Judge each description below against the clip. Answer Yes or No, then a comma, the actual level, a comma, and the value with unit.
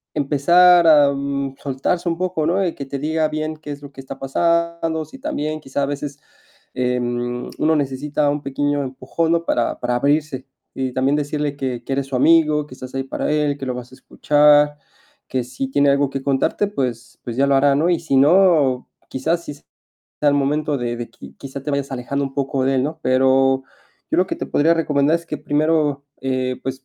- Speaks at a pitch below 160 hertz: Yes, medium, 140 Hz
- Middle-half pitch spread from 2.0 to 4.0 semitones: Yes, narrow, 2.5 semitones